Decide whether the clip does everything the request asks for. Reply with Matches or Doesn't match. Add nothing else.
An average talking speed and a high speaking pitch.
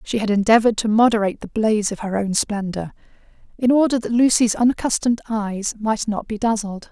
Matches